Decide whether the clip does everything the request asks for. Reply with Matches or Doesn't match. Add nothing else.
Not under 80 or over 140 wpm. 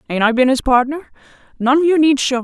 Doesn't match